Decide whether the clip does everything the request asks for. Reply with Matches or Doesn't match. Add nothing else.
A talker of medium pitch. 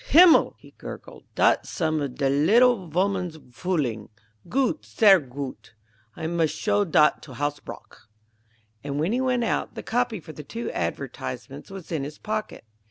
Matches